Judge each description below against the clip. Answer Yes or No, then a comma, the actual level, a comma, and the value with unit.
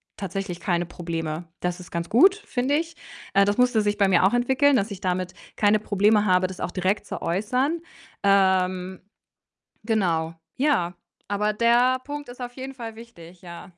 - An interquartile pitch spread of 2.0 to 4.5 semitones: No, average, 5.1 semitones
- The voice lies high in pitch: Yes, high, 205 Hz